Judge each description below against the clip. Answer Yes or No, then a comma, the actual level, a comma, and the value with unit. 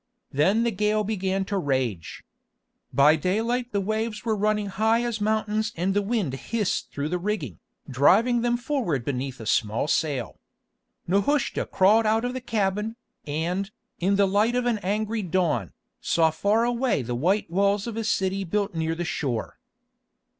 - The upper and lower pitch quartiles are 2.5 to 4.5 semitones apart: No, average, 5.3 semitones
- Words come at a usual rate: Yes, average, 165 wpm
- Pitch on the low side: No, high, 200 Hz